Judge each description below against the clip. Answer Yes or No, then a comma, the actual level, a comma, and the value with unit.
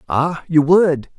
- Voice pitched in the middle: Yes, medium, 160 Hz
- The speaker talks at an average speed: Yes, average, 150 wpm